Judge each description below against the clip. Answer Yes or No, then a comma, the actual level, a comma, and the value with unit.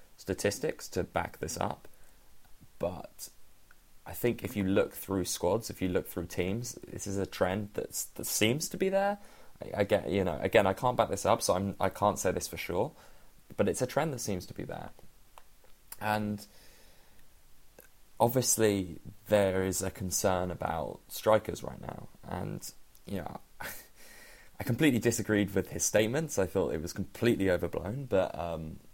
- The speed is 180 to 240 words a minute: No, average, 170 wpm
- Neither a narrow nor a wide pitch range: Yes, average, 3.5 semitones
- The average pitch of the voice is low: Yes, low, 105 Hz